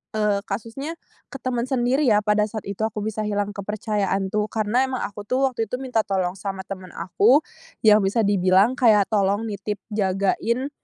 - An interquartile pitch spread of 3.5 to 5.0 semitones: No, average, 2.9 semitones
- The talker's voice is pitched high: Yes, high, 210 Hz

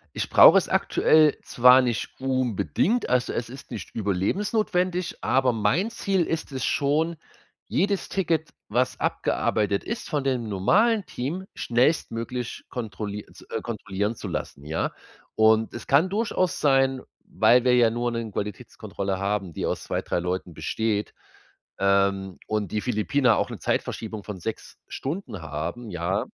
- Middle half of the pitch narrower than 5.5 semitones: No, wide, 6.3 semitones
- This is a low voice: Yes, low, 120 Hz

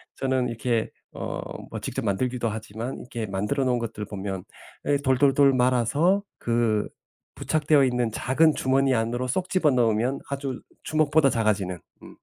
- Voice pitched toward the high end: No, low, 125 Hz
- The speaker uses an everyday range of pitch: Yes, average, 3.5 semitones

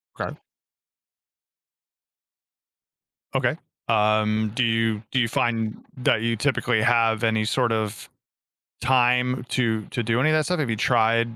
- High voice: No, low, 115 Hz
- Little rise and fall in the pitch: Yes, narrow, 2.2 semitones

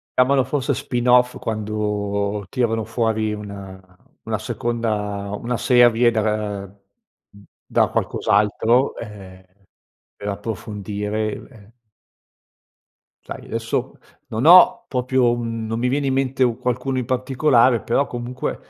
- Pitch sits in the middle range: No, low, 115 Hz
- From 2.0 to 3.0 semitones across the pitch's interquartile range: No, average, 3.4 semitones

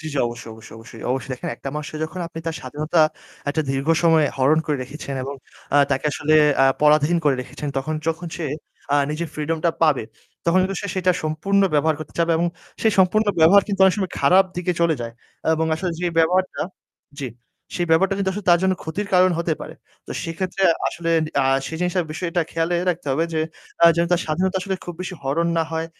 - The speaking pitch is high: No, medium, 165 Hz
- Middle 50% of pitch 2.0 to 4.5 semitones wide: Yes, average, 3.1 semitones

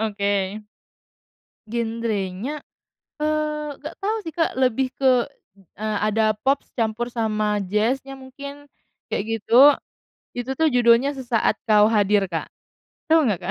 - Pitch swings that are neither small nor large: Yes, average, 4.6 semitones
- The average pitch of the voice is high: Yes, high, 235 Hz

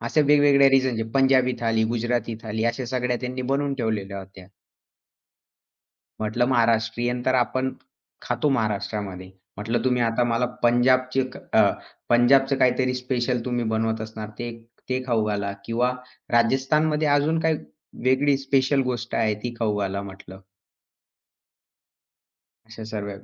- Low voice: Yes, low, 120 Hz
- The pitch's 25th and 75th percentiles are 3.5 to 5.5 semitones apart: No, average, 2.8 semitones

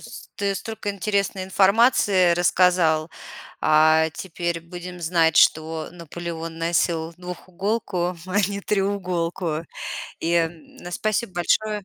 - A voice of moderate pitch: Yes, medium, 175 Hz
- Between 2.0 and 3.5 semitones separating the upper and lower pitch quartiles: Yes, average, 2.9 semitones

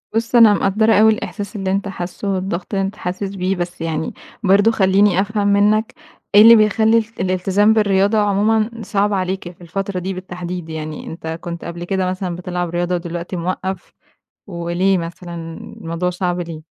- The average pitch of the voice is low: No, high, 190 Hz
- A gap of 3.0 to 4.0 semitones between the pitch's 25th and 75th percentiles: No, narrow, 2.6 semitones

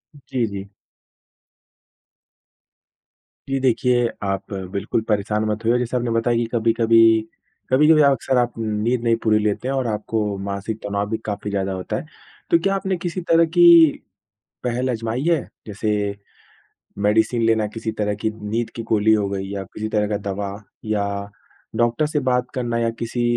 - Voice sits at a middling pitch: No, low, 115 Hz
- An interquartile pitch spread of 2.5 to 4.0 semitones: Yes, average, 2.9 semitones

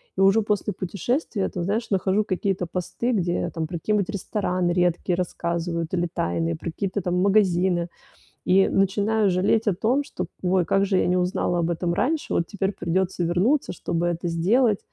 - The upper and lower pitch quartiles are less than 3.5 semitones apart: Yes, average, 2.8 semitones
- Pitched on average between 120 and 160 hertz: No, medium, 185 Hz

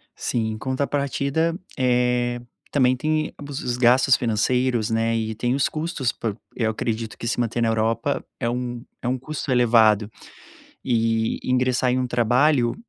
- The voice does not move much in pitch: Yes, narrow, 2.3 semitones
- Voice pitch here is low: Yes, low, 125 Hz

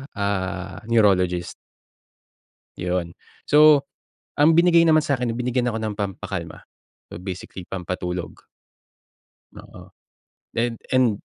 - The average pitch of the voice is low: Yes, low, 105 Hz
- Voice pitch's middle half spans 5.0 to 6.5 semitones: Yes, wide, 5.6 semitones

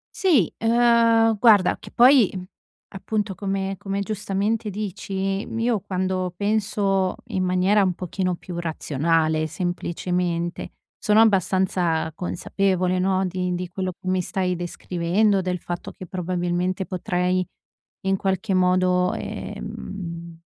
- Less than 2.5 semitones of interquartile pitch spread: Yes, narrow, 1.9 semitones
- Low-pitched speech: No, medium, 185 Hz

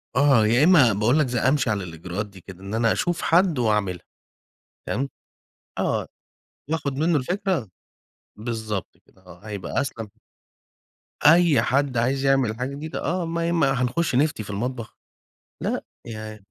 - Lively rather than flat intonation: Yes, wide, 5.7 semitones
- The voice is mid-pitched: No, low, 125 Hz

